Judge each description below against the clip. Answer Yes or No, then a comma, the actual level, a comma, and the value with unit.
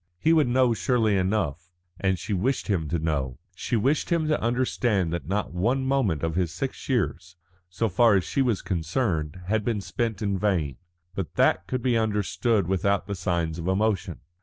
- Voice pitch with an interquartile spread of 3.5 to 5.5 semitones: Yes, average, 5.2 semitones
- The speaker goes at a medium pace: Yes, average, 185 wpm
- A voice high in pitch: No, low, 100 Hz